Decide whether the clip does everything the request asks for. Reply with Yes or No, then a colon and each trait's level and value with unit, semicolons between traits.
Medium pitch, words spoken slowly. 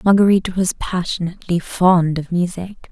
Yes: medium, 180 Hz; slow, 125 wpm